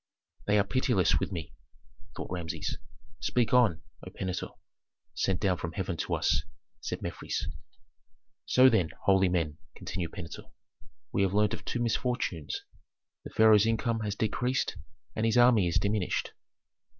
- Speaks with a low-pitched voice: Yes, low, 100 Hz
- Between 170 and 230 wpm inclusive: No, average, 145 wpm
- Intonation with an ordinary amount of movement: Yes, average, 4.2 semitones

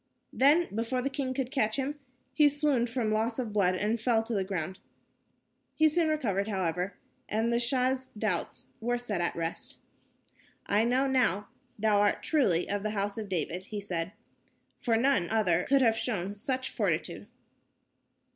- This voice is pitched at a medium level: No, high, 225 Hz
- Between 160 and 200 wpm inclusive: Yes, average, 165 wpm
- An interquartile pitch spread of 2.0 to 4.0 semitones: No, average, 4.5 semitones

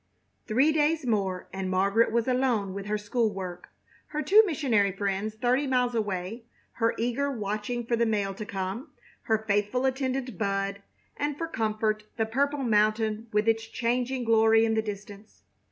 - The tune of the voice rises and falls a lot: No, average, 3.5 semitones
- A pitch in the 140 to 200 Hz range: No, high, 225 Hz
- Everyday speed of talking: Yes, average, 165 wpm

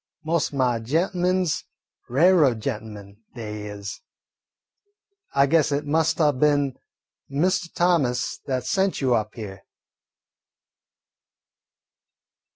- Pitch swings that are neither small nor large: No, wide, 6.1 semitones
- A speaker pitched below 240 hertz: Yes, medium, 140 Hz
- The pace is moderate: No, slow, 105 wpm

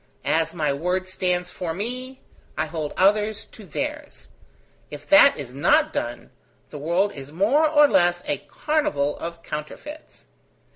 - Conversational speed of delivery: Yes, average, 145 wpm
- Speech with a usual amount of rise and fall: No, wide, 8.3 semitones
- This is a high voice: No, medium, 180 Hz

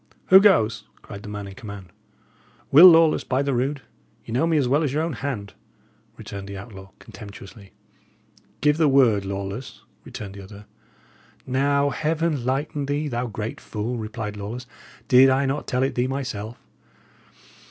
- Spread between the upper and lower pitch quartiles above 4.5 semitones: Yes, wide, 5.4 semitones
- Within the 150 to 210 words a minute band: Yes, average, 165 wpm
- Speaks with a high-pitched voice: No, low, 125 Hz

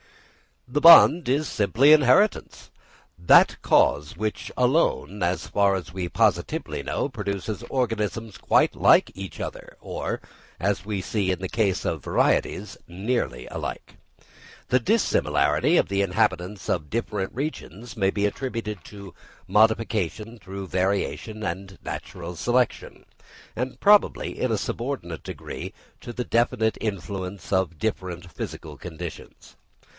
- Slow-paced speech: Yes, slow, 130 wpm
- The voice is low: Yes, low, 100 Hz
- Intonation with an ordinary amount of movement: Yes, average, 4.3 semitones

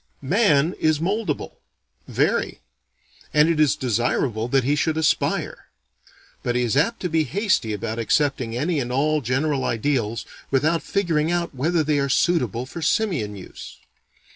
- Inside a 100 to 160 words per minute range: Yes, average, 150 wpm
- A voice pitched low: No, medium, 145 Hz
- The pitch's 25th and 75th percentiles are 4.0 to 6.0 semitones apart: Yes, average, 4.8 semitones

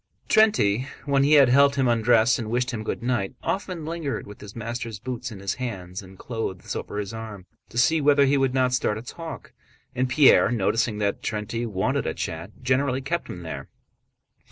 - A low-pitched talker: Yes, low, 120 Hz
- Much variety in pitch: No, average, 4.4 semitones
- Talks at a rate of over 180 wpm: Yes, average, 195 wpm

